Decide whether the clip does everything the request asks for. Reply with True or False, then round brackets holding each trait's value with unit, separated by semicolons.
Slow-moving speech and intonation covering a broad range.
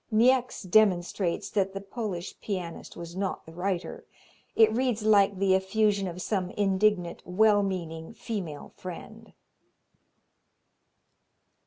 False (115 wpm; 3.1 semitones)